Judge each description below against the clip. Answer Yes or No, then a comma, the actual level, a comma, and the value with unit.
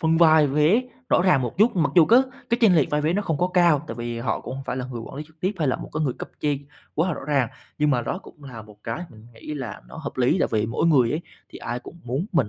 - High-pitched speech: No, medium, 150 Hz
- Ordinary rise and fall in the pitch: Yes, average, 4.9 semitones